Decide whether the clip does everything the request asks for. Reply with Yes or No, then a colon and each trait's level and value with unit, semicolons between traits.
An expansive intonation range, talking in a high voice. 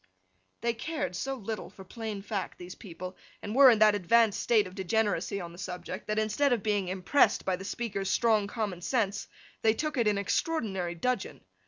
No: average, 3.4 semitones; high, 210 Hz